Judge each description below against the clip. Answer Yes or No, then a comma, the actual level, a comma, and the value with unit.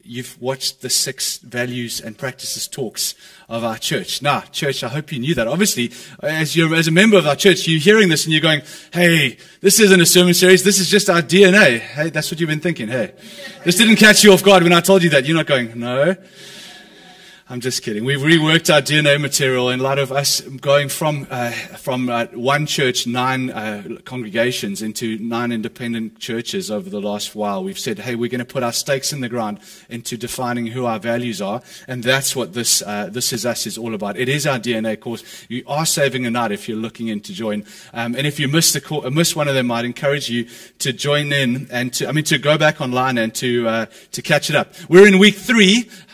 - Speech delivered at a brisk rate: Yes, fast, 230 wpm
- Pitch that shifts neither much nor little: No, wide, 7.4 semitones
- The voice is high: No, medium, 140 Hz